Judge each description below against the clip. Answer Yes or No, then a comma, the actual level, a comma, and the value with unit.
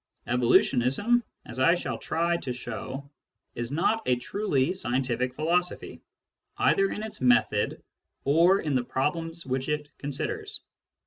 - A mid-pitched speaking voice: Yes, medium, 150 Hz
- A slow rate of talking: Yes, slow, 130 wpm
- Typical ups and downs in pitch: No, wide, 5.7 semitones